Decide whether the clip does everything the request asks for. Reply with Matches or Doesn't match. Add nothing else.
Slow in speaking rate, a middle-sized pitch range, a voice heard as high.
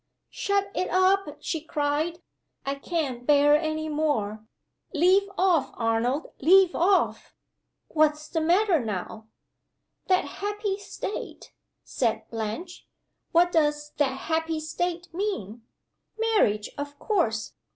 Matches